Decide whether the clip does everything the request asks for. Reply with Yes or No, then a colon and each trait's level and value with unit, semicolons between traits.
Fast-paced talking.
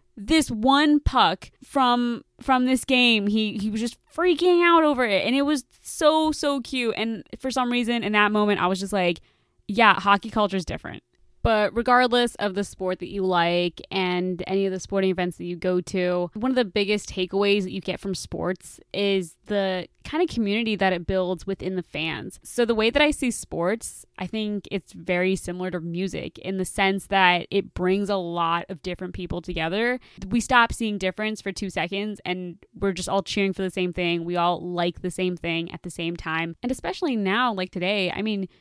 Yes: fast, 210 wpm